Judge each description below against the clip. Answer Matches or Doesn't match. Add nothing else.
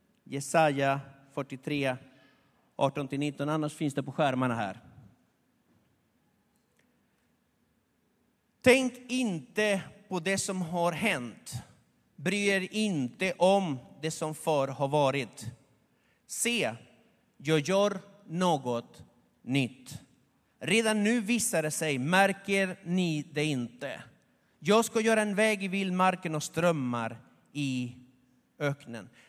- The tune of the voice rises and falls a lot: Matches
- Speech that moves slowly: Matches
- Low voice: Doesn't match